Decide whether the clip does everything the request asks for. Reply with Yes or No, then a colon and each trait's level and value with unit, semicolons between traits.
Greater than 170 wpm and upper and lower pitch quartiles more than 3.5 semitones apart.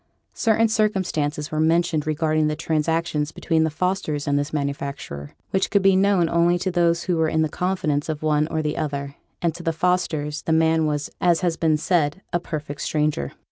No: average, 195 wpm; narrow, 2.5 semitones